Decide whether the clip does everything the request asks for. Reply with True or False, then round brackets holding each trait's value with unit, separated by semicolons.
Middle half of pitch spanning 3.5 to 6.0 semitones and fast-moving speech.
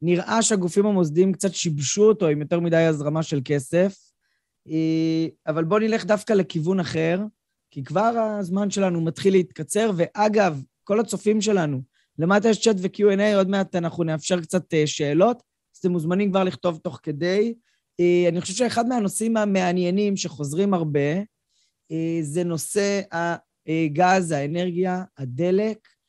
False (3.9 semitones; 130 wpm)